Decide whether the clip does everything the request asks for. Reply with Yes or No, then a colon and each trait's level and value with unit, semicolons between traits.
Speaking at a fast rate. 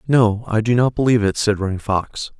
Yes: fast, 225 wpm